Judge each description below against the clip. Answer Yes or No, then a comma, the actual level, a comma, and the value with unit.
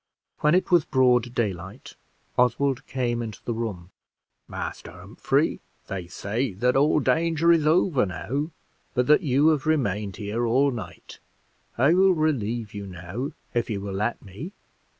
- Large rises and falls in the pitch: Yes, wide, 6.4 semitones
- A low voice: Yes, low, 125 Hz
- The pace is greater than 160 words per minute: No, average, 150 wpm